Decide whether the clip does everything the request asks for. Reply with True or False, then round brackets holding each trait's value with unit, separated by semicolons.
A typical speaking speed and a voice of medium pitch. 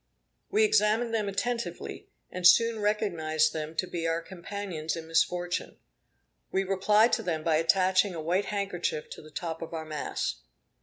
True (160 wpm; 180 Hz)